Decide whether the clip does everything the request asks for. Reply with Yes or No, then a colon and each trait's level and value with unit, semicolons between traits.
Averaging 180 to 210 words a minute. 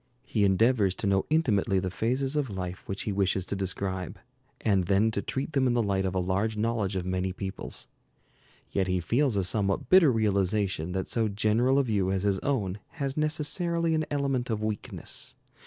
Yes: average, 190 wpm